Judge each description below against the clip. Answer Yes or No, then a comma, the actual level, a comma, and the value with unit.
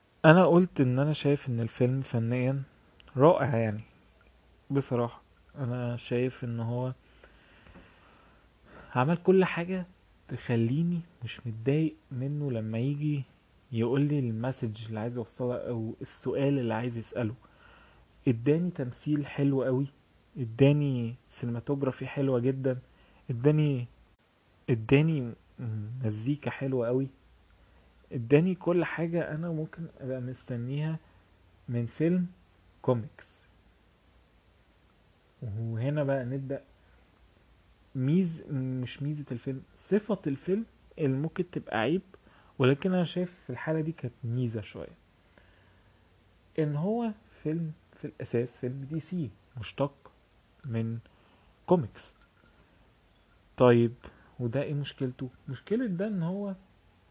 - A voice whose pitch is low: Yes, low, 130 Hz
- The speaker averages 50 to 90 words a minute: No, average, 105 wpm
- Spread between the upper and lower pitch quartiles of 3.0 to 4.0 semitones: No, average, 4.5 semitones